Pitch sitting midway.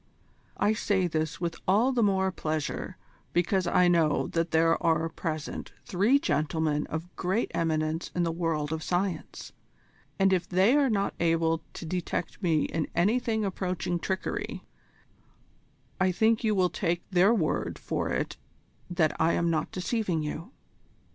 Yes: medium, 175 Hz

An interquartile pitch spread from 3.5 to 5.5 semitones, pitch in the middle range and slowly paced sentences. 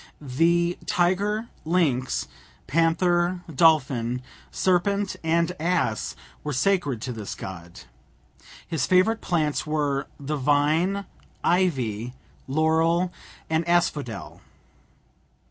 Yes: average, 4.4 semitones; medium, 160 Hz; slow, 90 wpm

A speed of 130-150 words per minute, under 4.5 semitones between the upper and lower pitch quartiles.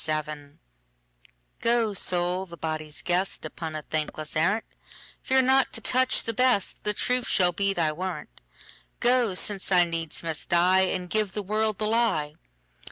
No: average, 140 wpm; average, 5.1 semitones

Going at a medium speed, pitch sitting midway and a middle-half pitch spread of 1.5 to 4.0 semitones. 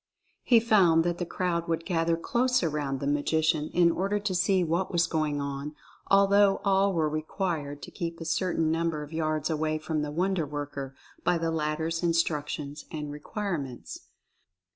Yes: average, 170 wpm; medium, 165 Hz; average, 3.0 semitones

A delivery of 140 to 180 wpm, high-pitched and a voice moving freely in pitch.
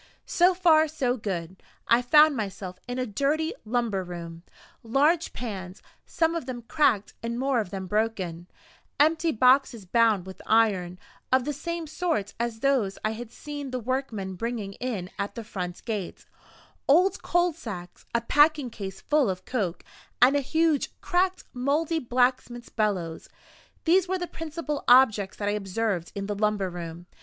Yes: average, 160 wpm; high, 235 Hz; wide, 6.9 semitones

